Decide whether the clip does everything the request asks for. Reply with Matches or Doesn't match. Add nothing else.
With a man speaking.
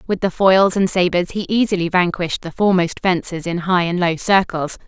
Doesn't match